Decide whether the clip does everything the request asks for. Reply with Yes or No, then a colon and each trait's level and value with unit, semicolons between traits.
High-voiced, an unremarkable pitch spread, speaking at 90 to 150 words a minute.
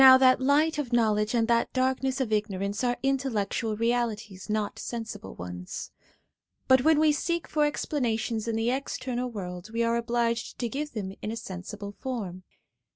No: high, 235 Hz; average, 3.6 semitones; average, 165 wpm